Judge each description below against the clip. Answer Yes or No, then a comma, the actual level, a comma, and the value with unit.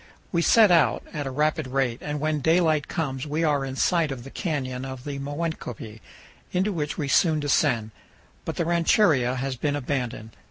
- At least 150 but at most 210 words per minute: Yes, average, 185 wpm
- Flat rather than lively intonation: No, average, 3.4 semitones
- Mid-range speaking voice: Yes, medium, 145 Hz